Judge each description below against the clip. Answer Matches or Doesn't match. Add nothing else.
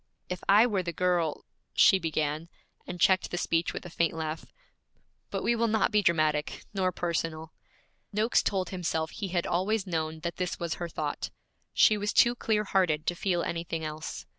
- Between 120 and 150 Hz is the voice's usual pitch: Doesn't match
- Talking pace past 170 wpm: Matches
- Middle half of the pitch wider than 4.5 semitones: Doesn't match